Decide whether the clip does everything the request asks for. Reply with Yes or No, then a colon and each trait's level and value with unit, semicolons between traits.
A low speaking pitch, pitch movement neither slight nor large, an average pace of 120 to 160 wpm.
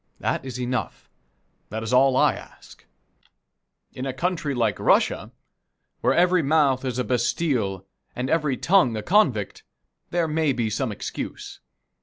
Yes: low, 130 Hz; average, 4.9 semitones; average, 145 wpm